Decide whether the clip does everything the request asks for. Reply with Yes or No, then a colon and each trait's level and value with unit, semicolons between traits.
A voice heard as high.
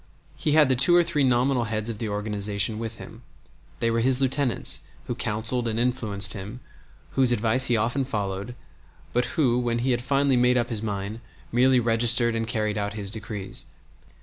No: low, 115 Hz